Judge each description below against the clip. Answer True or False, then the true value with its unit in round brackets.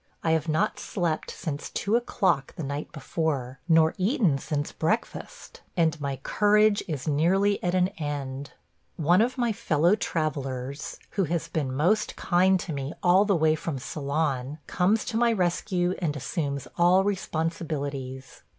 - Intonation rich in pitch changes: False (4.6 semitones)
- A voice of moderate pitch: True (160 Hz)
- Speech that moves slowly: False (150 wpm)